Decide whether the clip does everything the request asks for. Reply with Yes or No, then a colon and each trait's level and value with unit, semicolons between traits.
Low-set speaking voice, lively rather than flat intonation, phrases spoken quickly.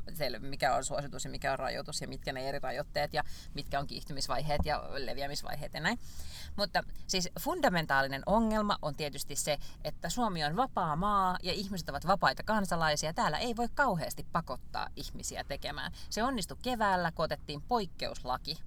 No: medium, 165 Hz; wide, 5.7 semitones; fast, 160 wpm